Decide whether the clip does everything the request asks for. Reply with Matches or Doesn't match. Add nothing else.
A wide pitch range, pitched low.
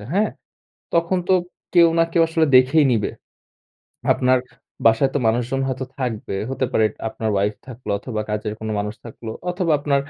Matches